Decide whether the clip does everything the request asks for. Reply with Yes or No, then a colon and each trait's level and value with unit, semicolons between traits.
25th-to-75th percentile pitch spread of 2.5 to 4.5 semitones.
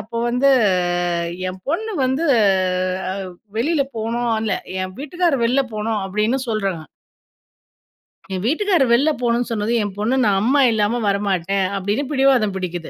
No: average, 5.1 semitones